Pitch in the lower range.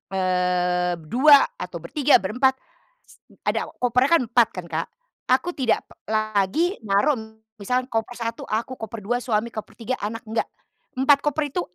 No: high, 230 Hz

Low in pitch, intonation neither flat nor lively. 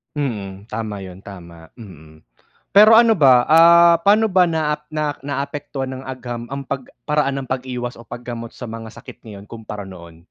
No: low, 125 Hz; wide, 6.0 semitones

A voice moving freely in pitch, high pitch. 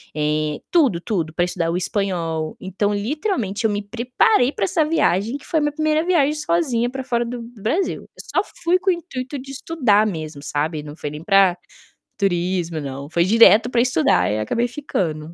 Yes: wide, 8.4 semitones; high, 205 Hz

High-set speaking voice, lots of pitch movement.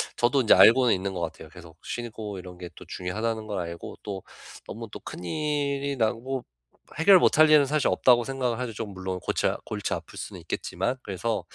No: low, 115 Hz; wide, 6.1 semitones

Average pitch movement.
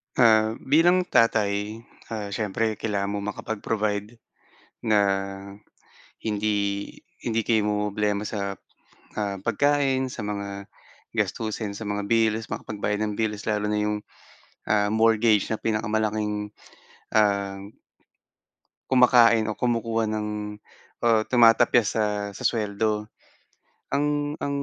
No: narrow, 1.7 semitones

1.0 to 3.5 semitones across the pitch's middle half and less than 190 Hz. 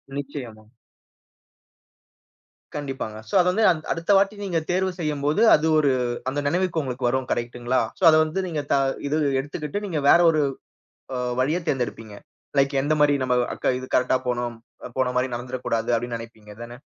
No: average, 4.2 semitones; medium, 140 Hz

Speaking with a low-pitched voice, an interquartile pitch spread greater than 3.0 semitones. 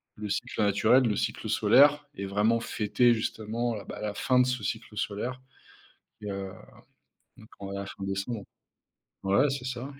Yes: low, 110 Hz; average, 3.8 semitones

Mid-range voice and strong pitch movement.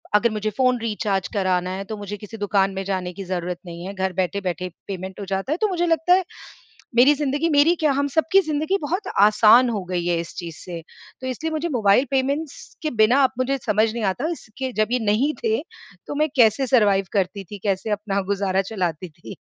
No: high, 215 Hz; wide, 6.4 semitones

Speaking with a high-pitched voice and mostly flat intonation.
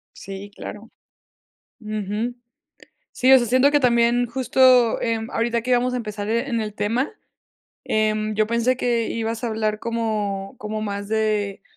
Yes: high, 225 Hz; narrow, 2.2 semitones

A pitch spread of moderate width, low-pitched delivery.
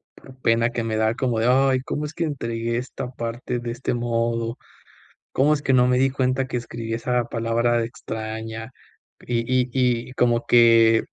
No: narrow, 1.8 semitones; low, 120 Hz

